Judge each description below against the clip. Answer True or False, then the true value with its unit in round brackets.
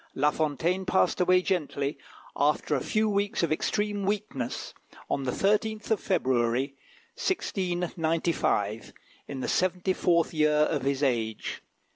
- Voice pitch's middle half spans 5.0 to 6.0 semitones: True (5.4 semitones)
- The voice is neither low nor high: True (165 Hz)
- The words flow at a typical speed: False (130 wpm)